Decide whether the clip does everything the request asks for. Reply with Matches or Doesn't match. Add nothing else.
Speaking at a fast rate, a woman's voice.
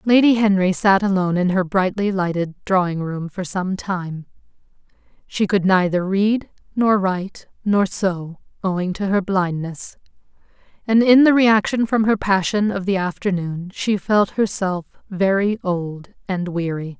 Doesn't match